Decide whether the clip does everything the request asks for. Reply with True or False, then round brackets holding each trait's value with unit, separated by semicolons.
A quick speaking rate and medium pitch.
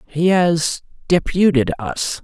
False (80 wpm; 160 Hz)